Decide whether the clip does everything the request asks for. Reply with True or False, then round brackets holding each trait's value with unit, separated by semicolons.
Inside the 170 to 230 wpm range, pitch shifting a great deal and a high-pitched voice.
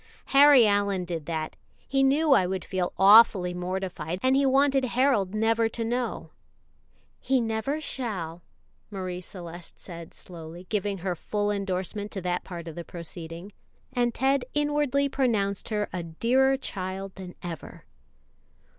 False (145 wpm; 6.0 semitones; 200 Hz)